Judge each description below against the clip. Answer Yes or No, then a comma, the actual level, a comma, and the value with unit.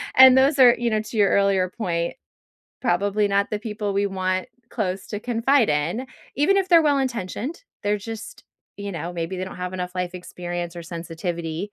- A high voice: Yes, high, 200 Hz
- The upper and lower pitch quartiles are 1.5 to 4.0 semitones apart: No, average, 4.5 semitones